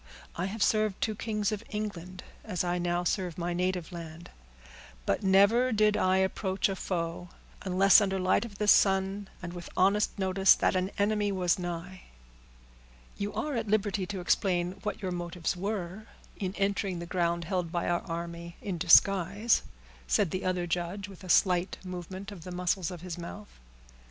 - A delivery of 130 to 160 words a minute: No, average, 175 wpm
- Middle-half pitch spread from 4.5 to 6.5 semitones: No, narrow, 2.5 semitones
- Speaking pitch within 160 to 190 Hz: Yes, medium, 185 Hz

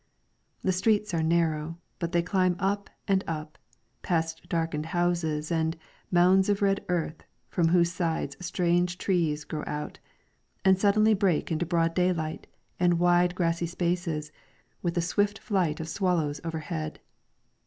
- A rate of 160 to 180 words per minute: No, average, 145 wpm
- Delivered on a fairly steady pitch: Yes, narrow, 2.2 semitones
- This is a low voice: No, medium, 175 Hz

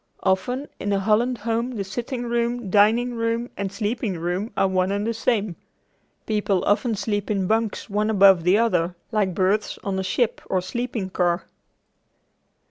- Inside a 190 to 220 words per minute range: No, average, 165 wpm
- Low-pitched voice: No, high, 210 Hz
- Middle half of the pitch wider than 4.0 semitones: No, average, 3.4 semitones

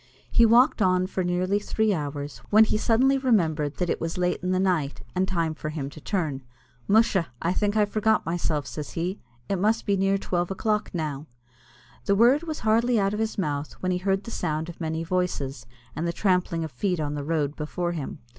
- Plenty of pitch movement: No, average, 4.8 semitones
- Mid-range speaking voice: Yes, medium, 180 Hz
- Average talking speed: No, fast, 210 wpm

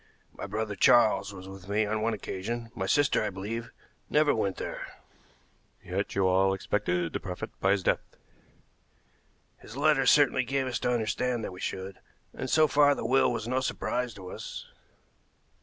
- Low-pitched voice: Yes, low, 110 Hz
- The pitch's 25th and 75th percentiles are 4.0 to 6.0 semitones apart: Yes, average, 4.6 semitones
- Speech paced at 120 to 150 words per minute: No, average, 175 wpm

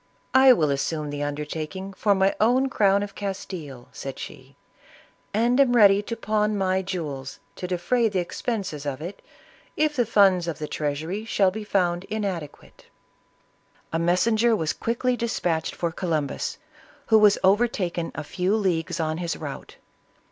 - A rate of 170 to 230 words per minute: No, average, 160 wpm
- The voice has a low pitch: No, high, 190 Hz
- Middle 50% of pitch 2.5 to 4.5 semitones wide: No, average, 5.0 semitones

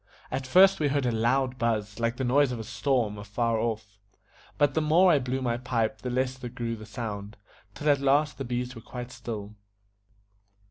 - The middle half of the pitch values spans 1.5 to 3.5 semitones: Yes, average, 3.1 semitones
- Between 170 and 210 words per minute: Yes, average, 195 wpm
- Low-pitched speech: Yes, low, 125 Hz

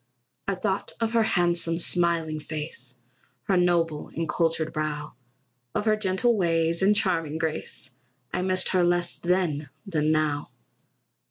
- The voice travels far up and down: No, average, 3.1 semitones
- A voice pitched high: No, medium, 170 Hz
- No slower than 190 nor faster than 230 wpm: No, average, 140 wpm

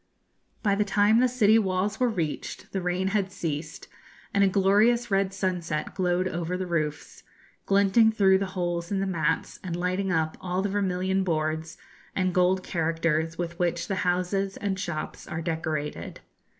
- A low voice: No, medium, 185 Hz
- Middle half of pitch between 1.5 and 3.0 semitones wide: Yes, average, 2.7 semitones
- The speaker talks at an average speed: Yes, average, 165 wpm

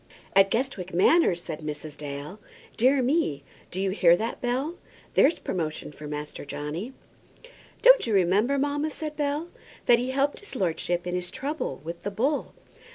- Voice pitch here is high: Yes, high, 200 Hz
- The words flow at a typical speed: Yes, average, 160 wpm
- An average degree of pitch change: No, wide, 8.8 semitones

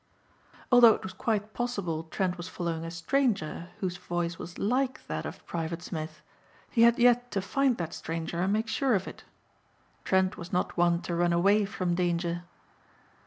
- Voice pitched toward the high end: No, medium, 180 Hz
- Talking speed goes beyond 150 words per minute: Yes, average, 175 wpm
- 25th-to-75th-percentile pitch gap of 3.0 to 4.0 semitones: No, average, 4.5 semitones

